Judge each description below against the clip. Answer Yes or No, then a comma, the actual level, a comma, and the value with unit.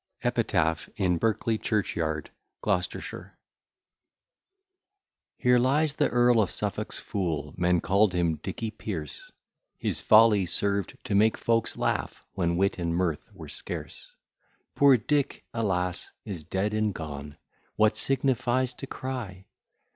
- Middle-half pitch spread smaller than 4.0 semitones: No, average, 4.9 semitones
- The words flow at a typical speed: No, slow, 125 wpm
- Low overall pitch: Yes, low, 100 Hz